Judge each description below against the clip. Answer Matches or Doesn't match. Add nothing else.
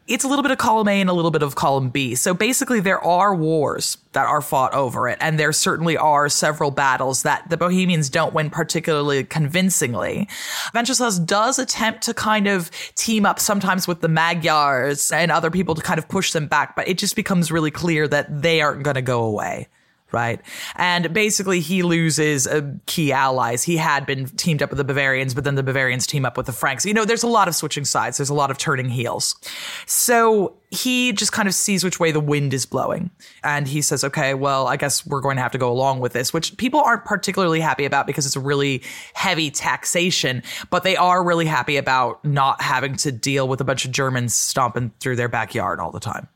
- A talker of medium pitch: Matches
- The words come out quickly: Matches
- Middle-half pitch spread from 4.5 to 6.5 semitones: Matches